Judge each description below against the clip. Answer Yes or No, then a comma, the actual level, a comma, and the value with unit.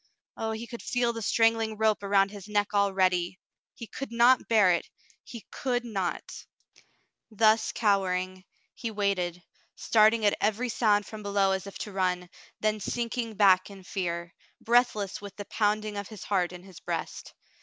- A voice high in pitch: Yes, high, 205 Hz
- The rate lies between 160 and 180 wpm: Yes, average, 165 wpm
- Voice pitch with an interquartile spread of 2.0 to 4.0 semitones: Yes, average, 2.8 semitones